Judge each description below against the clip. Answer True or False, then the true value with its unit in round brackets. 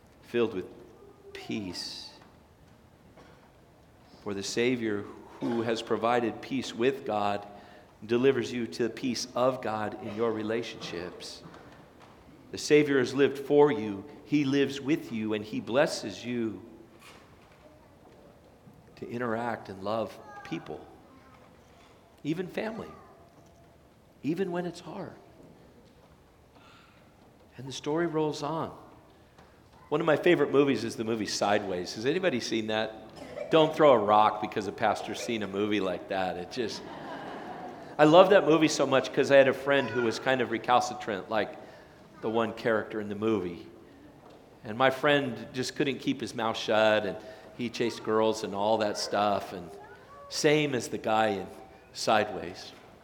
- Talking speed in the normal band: True (145 wpm)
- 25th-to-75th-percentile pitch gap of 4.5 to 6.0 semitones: True (4.8 semitones)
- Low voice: True (115 Hz)